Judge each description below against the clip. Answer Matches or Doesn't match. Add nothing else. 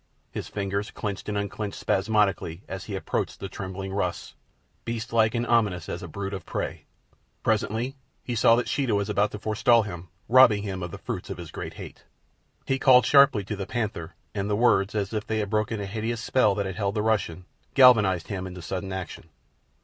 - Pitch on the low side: Matches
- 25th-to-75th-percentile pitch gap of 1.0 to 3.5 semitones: Matches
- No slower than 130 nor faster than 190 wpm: Doesn't match